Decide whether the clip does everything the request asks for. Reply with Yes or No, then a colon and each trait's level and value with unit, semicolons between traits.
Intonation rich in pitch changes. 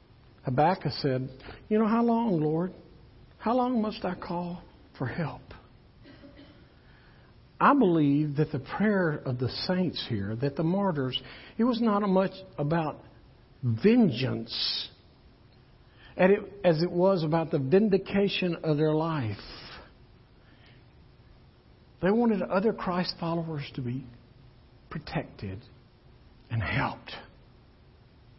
Yes: wide, 7.0 semitones